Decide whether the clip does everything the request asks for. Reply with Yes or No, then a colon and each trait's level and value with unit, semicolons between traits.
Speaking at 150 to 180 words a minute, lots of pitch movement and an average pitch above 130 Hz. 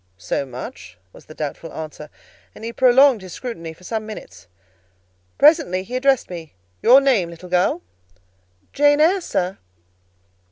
No: slow, 135 wpm; wide, 8.4 semitones; medium, 185 Hz